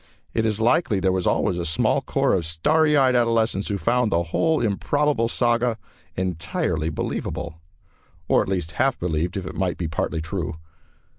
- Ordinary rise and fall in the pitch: No, wide, 5.8 semitones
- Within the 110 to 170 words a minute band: Yes, average, 165 wpm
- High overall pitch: No, very low, 95 Hz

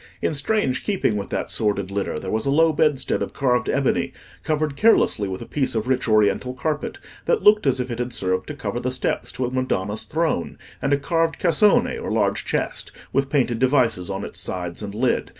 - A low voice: Yes, low, 130 Hz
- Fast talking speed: Yes, fast, 210 wpm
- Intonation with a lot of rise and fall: Yes, wide, 5.7 semitones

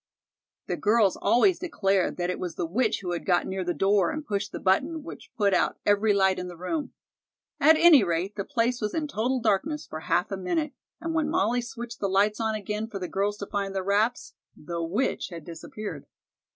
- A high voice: Yes, high, 205 Hz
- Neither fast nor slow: No, fast, 215 wpm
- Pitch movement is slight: No, average, 4.5 semitones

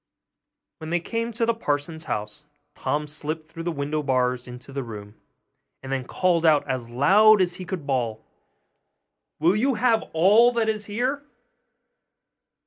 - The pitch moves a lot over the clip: Yes, wide, 7.8 semitones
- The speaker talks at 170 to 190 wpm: No, average, 155 wpm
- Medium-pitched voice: Yes, medium, 160 Hz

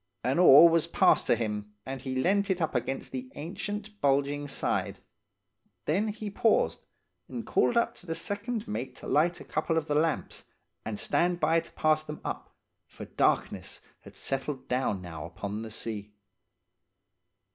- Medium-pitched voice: Yes, medium, 150 Hz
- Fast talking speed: No, average, 165 wpm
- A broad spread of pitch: Yes, wide, 5.7 semitones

